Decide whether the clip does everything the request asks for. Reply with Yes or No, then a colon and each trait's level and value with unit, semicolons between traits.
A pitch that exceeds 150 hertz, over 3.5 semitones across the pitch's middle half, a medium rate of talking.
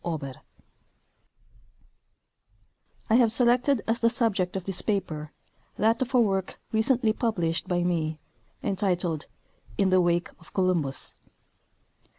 No: high, 190 Hz; average, 4.7 semitones; slow, 130 wpm